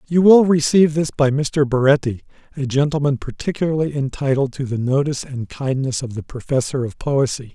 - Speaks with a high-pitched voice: No, medium, 140 Hz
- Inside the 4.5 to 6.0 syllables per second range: Yes, 5.5 syllables/s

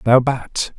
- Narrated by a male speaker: Yes, male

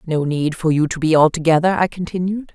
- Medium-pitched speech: Yes, medium, 165 Hz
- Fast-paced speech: Yes, fast, 210 wpm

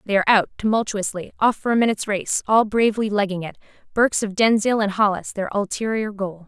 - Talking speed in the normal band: Yes, average, 195 wpm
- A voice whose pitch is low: No, high, 205 Hz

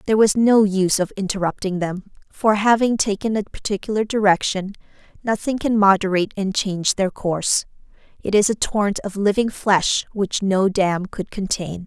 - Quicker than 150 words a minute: Yes, average, 160 wpm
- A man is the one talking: No, female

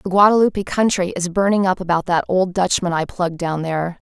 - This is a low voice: No, medium, 180 Hz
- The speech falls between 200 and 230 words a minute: Yes, fast, 205 wpm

